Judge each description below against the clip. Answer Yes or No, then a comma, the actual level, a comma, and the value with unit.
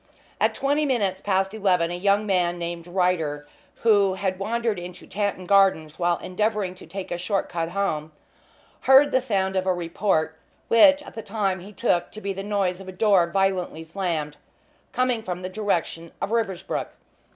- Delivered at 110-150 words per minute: No, average, 175 wpm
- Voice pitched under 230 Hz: Yes, high, 190 Hz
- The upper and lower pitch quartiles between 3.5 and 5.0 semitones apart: No, average, 3.0 semitones